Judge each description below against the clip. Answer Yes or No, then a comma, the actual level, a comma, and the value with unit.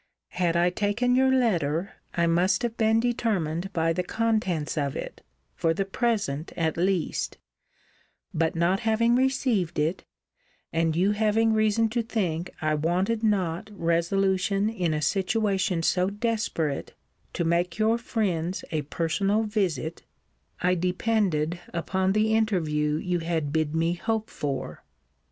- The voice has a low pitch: No, medium, 185 Hz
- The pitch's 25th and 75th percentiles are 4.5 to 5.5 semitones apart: Yes, average, 4.8 semitones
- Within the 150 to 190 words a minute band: No, slow, 135 wpm